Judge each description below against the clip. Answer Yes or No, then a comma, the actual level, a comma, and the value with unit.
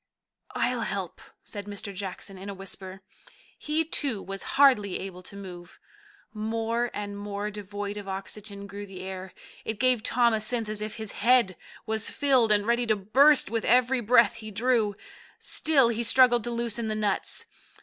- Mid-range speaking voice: No, high, 215 Hz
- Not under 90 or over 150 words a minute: No, average, 170 wpm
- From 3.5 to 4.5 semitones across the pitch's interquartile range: No, average, 2.9 semitones